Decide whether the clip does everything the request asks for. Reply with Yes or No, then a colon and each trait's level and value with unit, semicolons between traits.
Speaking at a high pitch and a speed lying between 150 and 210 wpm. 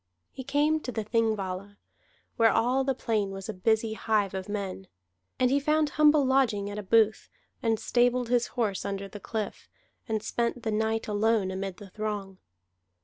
Yes: high, 220 Hz; average, 175 wpm